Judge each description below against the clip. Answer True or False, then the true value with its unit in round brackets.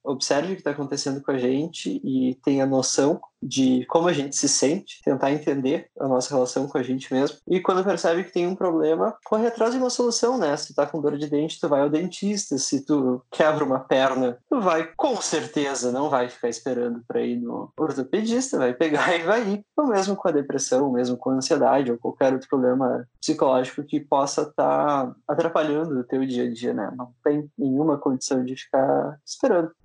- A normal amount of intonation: True (4.3 semitones)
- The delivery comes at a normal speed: False (210 wpm)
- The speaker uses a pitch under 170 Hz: True (140 Hz)